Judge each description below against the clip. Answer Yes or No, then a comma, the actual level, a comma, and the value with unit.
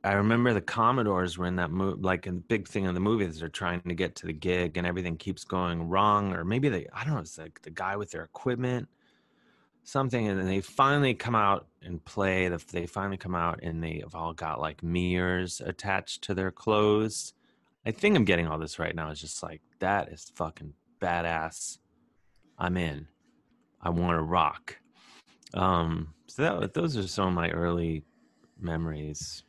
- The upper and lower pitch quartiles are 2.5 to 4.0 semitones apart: Yes, average, 3.1 semitones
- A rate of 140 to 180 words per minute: No, average, 195 wpm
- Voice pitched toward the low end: Yes, very low, 90 Hz